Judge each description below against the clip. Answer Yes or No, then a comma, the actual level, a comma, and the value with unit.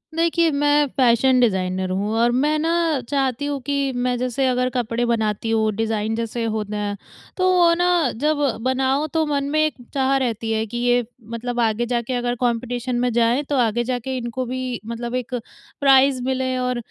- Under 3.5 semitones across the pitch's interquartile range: Yes, average, 2.7 semitones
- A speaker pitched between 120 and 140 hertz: No, high, 245 Hz